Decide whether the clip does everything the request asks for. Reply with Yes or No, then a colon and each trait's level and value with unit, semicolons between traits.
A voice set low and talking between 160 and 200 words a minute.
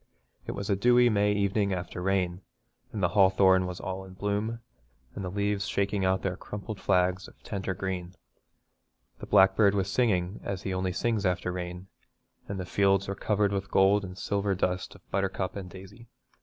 Yes: very low, 95 Hz; average, 185 wpm